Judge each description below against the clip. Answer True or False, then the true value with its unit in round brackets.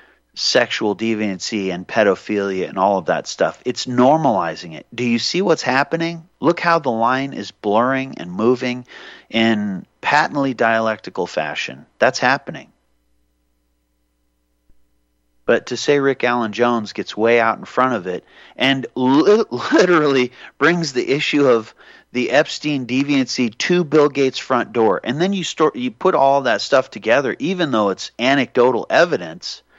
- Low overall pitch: True (125 Hz)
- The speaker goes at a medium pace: True (150 wpm)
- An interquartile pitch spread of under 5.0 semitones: False (5.4 semitones)